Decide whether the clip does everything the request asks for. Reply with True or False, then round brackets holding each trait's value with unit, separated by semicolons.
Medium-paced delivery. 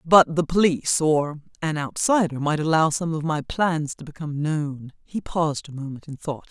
True (195 wpm)